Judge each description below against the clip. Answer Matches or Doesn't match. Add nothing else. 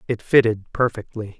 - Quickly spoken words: Doesn't match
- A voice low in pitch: Matches